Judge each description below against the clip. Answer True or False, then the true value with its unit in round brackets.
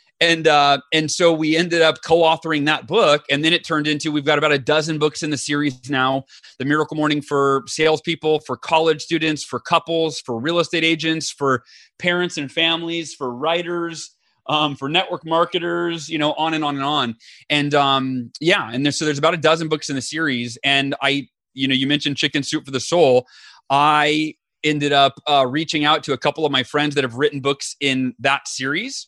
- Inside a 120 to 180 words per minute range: False (205 wpm)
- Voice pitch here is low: False (150 Hz)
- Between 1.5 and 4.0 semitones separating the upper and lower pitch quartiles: True (2.5 semitones)